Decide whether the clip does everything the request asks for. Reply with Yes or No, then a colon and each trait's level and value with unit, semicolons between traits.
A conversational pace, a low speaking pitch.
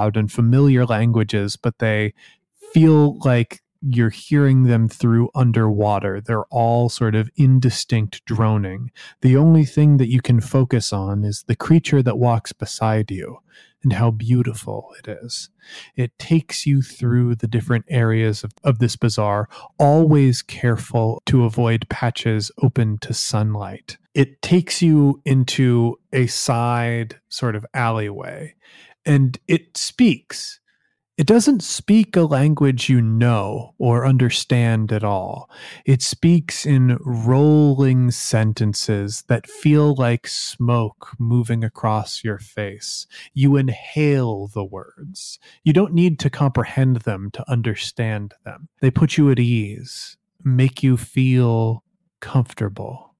No: slow, 130 wpm; low, 120 Hz